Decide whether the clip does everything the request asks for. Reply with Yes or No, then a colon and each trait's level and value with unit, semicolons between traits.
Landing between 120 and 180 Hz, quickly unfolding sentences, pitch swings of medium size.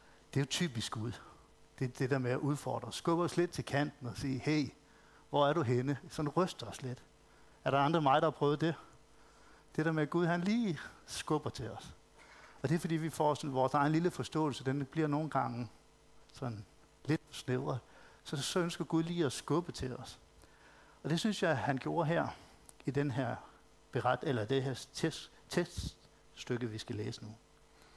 No: medium, 140 Hz; average, 200 wpm; average, 4.1 semitones